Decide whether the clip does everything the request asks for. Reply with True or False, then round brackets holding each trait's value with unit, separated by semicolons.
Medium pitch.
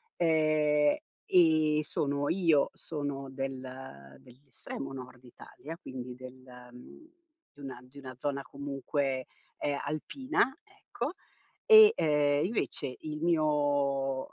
True (145 Hz)